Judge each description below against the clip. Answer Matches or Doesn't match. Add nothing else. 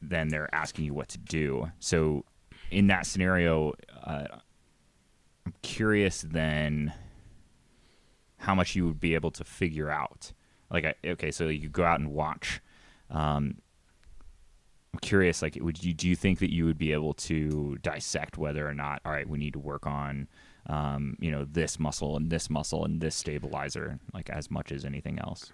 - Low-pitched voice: Matches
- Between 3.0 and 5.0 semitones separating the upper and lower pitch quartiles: Doesn't match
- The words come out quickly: Doesn't match